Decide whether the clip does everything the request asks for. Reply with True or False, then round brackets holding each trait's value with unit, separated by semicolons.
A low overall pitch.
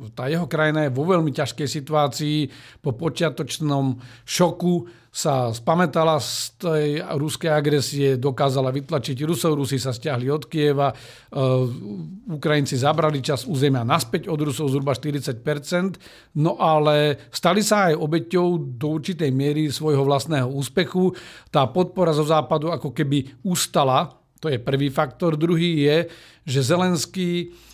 False (150 Hz)